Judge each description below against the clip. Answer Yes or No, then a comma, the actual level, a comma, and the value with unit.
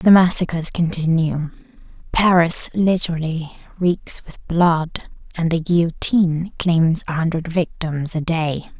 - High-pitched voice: No, medium, 165 Hz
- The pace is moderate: No, slow, 115 wpm